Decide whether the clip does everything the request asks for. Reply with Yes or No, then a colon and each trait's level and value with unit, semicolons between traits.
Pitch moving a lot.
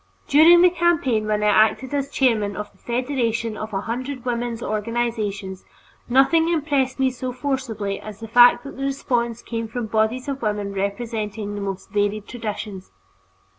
No: average, 3.9 semitones